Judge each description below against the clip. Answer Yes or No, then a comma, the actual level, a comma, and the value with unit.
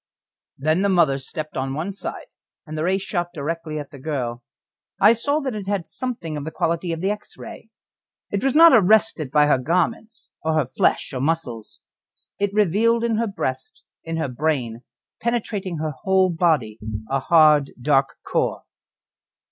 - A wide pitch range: Yes, wide, 5.7 semitones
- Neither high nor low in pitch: Yes, medium, 165 Hz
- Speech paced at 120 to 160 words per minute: No, average, 170 wpm